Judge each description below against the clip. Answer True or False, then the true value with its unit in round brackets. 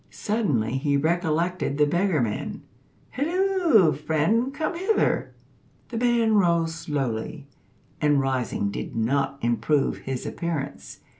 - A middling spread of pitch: False (8.1 semitones)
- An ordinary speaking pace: False (115 wpm)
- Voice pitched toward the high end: False (160 Hz)